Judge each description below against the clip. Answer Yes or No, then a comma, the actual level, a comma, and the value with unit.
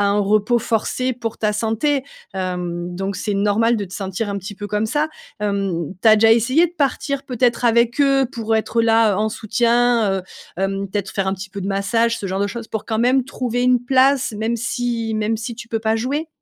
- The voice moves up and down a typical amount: Yes, average, 3.3 semitones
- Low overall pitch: No, high, 225 Hz